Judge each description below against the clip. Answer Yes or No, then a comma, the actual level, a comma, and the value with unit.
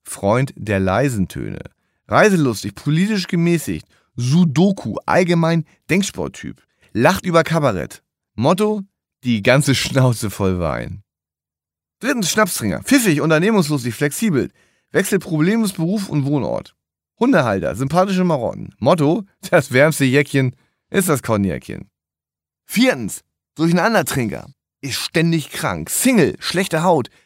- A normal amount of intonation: No, wide, 7.8 semitones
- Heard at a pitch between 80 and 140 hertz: No, medium, 155 Hz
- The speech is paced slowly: Yes, slow, 105 wpm